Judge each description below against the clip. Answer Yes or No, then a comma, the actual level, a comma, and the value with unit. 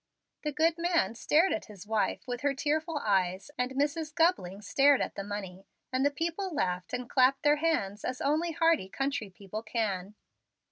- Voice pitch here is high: Yes, very high, 265 Hz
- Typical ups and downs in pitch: No, wide, 7.5 semitones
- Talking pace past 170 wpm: Yes, average, 180 wpm